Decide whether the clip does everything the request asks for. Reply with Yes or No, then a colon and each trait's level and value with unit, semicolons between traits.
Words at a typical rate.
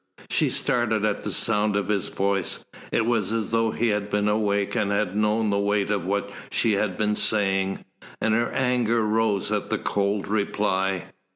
Yes: average, 185 wpm